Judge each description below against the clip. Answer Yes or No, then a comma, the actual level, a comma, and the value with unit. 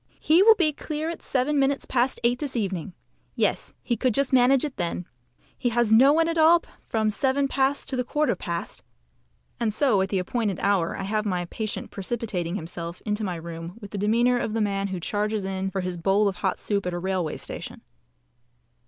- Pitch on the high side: Yes, high, 215 Hz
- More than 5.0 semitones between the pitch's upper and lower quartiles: Yes, wide, 5.6 semitones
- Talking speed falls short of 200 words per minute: No, fast, 205 wpm